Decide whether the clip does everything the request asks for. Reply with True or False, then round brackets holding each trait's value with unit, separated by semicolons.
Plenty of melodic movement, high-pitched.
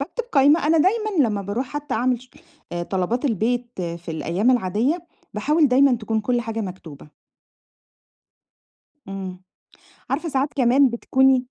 True (5.7 semitones; 245 Hz)